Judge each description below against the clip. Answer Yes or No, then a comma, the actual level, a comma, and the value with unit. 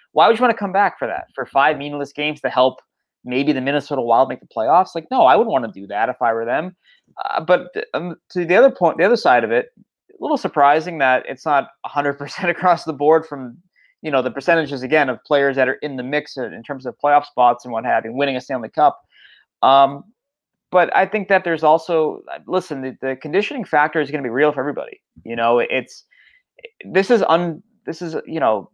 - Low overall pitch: No, medium, 150 Hz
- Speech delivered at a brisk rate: Yes, fast, 235 wpm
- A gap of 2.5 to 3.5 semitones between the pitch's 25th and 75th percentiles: No, wide, 5.5 semitones